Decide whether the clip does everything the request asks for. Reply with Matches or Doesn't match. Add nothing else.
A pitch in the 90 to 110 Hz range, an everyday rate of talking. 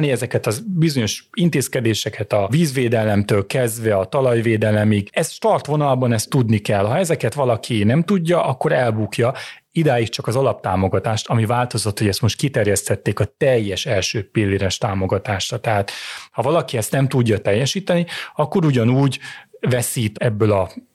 Doesn't match